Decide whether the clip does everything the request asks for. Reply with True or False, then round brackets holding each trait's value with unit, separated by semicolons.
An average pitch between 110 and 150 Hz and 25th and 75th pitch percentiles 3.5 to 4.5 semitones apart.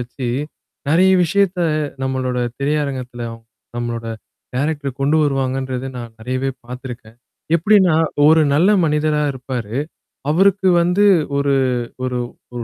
True (135 Hz; 4.1 semitones)